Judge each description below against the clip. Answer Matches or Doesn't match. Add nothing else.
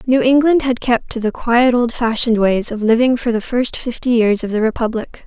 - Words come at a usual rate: Doesn't match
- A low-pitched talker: Doesn't match